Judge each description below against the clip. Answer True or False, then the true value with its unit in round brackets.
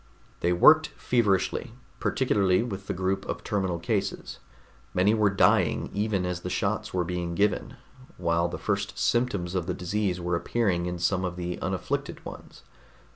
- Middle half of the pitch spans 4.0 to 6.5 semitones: False (2.9 semitones)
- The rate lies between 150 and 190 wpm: True (160 wpm)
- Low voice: True (95 Hz)